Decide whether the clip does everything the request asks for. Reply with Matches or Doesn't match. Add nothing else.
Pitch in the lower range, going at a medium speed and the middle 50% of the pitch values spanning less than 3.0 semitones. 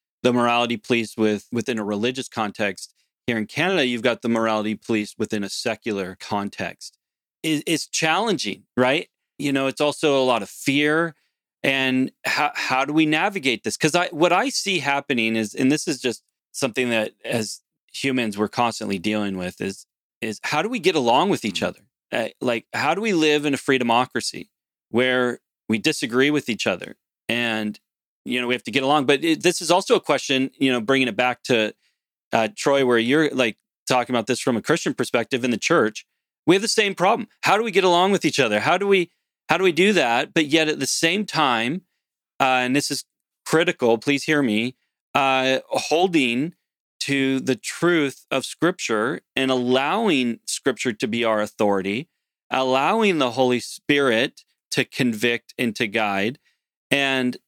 Doesn't match